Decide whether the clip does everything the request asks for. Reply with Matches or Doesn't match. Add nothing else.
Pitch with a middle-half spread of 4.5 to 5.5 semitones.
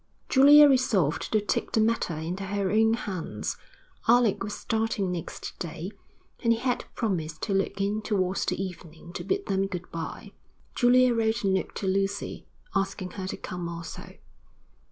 Doesn't match